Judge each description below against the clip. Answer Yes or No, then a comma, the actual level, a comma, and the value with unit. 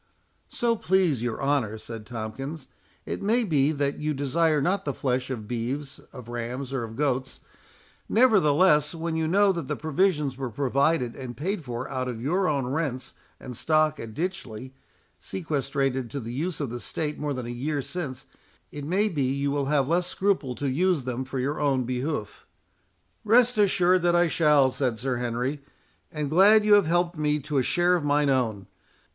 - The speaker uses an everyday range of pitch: Yes, average, 4.6 semitones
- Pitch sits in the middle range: Yes, medium, 145 Hz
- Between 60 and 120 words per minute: No, average, 185 wpm